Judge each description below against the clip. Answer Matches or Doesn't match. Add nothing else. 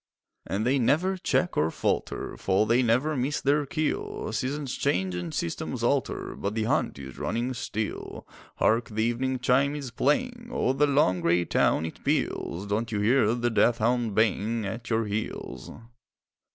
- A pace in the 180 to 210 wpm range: Doesn't match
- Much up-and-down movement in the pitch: Doesn't match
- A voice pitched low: Matches